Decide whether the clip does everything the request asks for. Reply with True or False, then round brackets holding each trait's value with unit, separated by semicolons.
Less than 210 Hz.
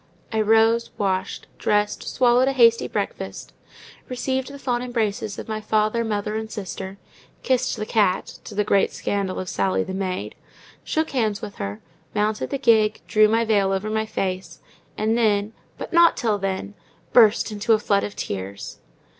False (215 Hz)